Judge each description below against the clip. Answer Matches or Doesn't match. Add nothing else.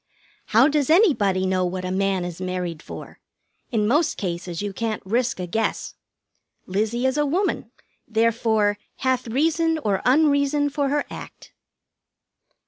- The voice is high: Matches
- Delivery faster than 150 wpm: Doesn't match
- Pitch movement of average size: Doesn't match